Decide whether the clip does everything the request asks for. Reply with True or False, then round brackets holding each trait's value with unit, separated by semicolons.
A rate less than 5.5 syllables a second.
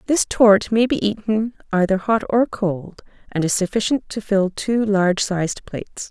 True (4.7 syllables/s)